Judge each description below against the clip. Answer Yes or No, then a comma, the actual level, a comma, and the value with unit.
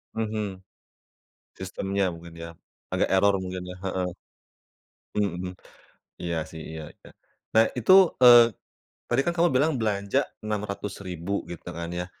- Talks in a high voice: No, very low, 95 Hz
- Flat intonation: No, average, 3.6 semitones